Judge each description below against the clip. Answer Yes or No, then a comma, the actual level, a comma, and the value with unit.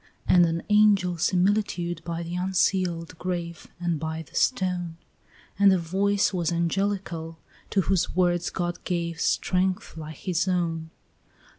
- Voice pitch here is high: No, medium, 175 Hz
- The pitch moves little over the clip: Yes, narrow, 2.0 semitones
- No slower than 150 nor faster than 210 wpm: No, slow, 135 wpm